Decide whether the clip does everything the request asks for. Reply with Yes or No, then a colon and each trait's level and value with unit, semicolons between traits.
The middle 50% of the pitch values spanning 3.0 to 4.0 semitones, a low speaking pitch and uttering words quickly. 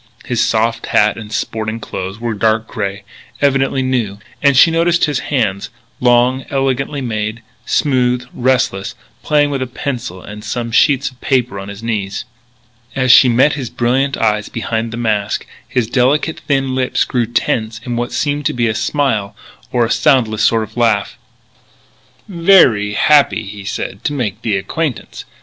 No: average, 3.7 semitones; low, 120 Hz; average, 165 wpm